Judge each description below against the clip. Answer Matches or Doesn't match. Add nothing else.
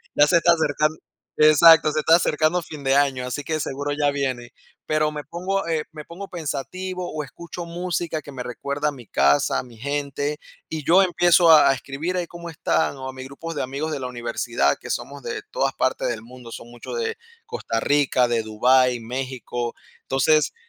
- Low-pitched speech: Doesn't match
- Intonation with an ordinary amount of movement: Matches